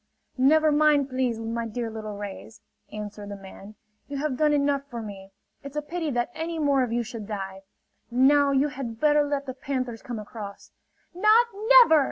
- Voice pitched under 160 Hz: No, very high, 255 Hz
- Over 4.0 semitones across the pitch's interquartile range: Yes, average, 5.1 semitones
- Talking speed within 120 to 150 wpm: No, average, 185 wpm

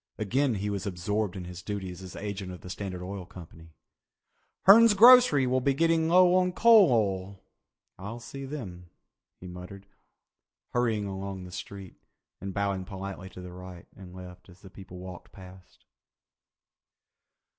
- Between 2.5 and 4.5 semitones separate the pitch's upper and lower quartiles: No, average, 5.0 semitones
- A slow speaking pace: No, average, 155 wpm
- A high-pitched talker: No, low, 100 Hz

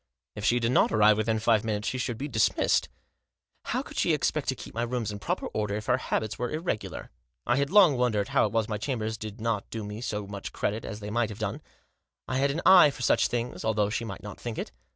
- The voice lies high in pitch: No, low, 110 Hz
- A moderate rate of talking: No, fast, 250 wpm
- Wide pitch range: No, narrow, 2.6 semitones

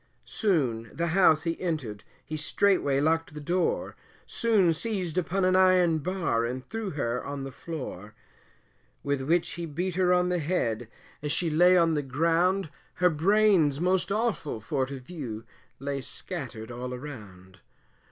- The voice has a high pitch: No, medium, 160 Hz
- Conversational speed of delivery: Yes, average, 160 wpm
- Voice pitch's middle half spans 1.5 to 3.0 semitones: No, wide, 5.4 semitones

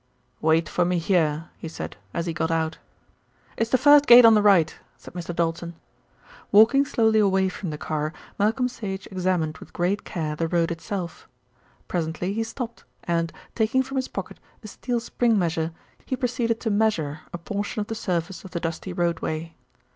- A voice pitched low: No, medium, 185 Hz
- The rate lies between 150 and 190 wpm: Yes, average, 180 wpm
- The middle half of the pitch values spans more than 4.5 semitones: Yes, average, 5.1 semitones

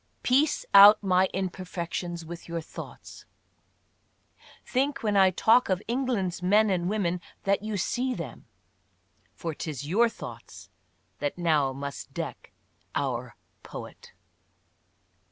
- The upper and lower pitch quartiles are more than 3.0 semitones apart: Yes, average, 4.2 semitones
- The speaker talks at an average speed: No, slow, 120 wpm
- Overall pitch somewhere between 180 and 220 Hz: Yes, medium, 185 Hz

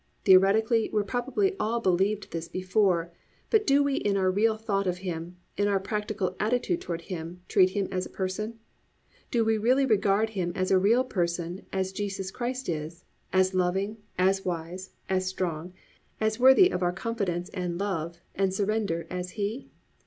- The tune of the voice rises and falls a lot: No, average, 3.2 semitones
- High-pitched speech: Yes, high, 195 Hz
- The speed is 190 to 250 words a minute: No, average, 170 wpm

